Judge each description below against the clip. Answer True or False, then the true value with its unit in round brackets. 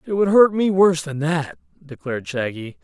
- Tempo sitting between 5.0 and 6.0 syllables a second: True (5.2 syllables/s)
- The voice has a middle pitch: True (155 Hz)